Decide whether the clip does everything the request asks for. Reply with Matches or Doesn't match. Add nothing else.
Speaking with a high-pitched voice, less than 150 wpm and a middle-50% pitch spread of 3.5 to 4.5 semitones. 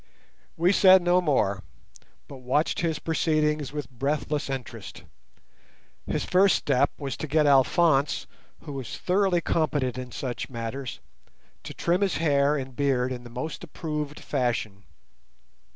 Doesn't match